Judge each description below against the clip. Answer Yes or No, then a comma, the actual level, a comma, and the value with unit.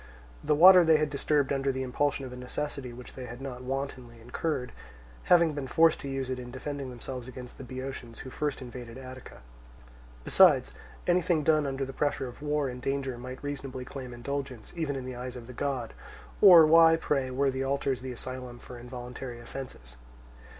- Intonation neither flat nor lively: No, narrow, 2.3 semitones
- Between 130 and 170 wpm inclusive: No, average, 190 wpm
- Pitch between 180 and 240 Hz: No, low, 130 Hz